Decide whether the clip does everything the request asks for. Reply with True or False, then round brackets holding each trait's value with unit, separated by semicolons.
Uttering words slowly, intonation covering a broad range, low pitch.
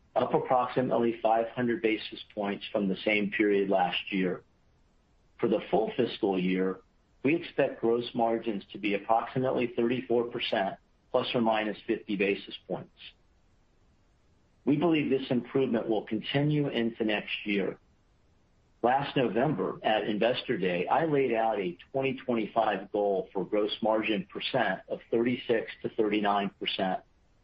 False (125 wpm; 3.2 semitones; 110 Hz)